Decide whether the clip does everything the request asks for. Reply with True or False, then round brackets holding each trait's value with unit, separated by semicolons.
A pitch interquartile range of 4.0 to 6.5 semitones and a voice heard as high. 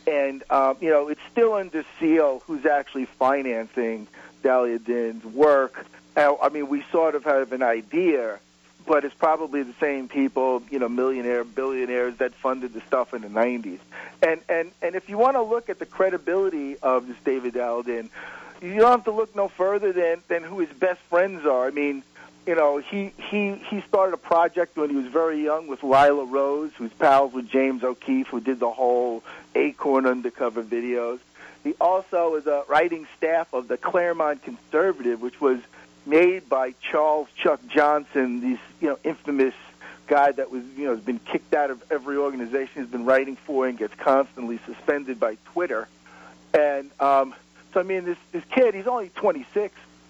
False (5.0 semitones; 140 Hz)